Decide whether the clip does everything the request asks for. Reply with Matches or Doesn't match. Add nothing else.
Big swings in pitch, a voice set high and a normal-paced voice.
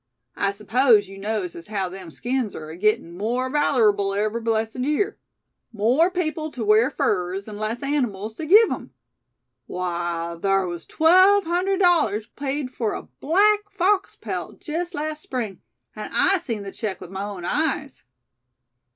Matches